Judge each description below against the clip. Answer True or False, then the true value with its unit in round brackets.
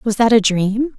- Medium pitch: False (220 Hz)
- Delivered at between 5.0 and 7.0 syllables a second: False (4.4 syllables/s)